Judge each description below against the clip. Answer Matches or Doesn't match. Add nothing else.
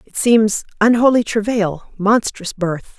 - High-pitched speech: Matches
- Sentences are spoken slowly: Matches